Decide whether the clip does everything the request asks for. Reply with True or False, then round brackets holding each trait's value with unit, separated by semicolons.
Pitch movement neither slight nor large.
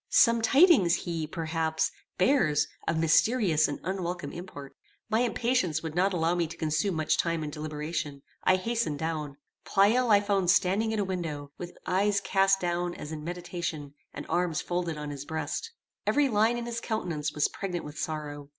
True (4.4 semitones)